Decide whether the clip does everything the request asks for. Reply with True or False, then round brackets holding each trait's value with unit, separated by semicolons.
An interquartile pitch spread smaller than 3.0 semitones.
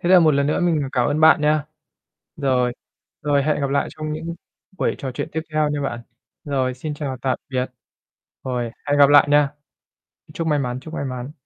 True (2.6 semitones)